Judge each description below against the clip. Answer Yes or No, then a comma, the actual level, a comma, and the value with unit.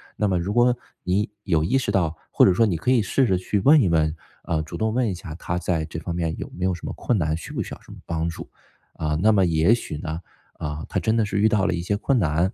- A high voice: No, very low, 90 Hz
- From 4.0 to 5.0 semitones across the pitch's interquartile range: Yes, average, 4.7 semitones